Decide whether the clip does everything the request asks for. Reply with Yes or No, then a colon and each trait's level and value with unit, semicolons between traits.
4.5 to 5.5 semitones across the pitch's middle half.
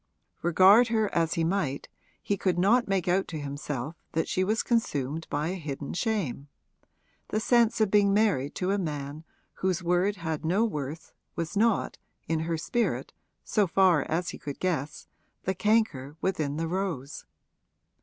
Yes: average, 4.8 semitones